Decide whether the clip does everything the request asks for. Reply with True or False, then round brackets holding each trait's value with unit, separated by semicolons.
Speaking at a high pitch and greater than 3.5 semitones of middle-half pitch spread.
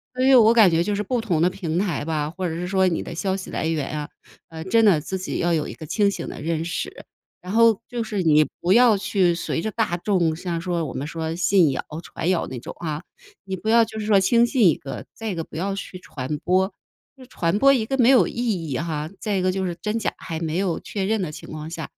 False (180 Hz; 4.3 semitones)